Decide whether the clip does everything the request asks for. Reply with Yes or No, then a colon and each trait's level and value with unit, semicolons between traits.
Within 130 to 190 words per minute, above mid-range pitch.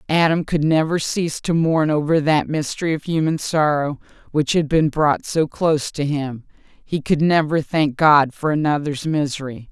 No: average, 175 wpm; medium, 150 Hz